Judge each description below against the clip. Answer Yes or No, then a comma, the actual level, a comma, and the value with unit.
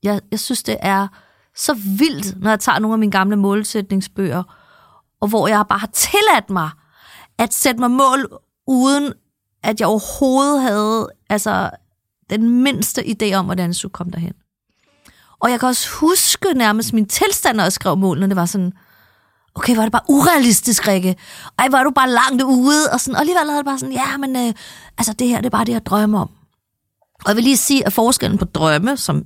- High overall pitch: Yes, high, 220 Hz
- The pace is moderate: Yes, average, 205 wpm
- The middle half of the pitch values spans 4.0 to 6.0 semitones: Yes, average, 5.1 semitones